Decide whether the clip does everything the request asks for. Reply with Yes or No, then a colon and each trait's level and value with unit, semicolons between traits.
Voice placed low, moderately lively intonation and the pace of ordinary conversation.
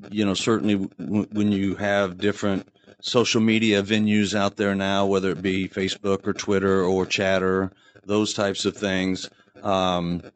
No: low, 100 Hz; narrow, 1.3 semitones; average, 155 wpm